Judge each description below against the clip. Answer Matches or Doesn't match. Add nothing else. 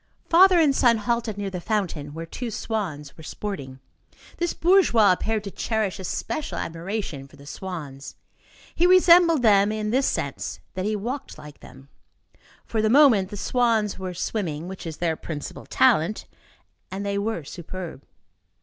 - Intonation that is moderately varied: Doesn't match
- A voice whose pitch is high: Matches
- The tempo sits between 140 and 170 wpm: Matches